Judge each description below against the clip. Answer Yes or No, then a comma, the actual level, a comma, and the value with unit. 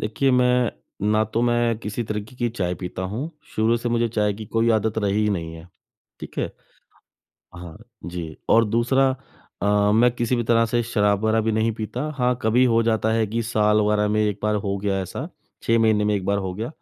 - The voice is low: Yes, low, 110 Hz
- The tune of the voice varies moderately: No, narrow, 2.3 semitones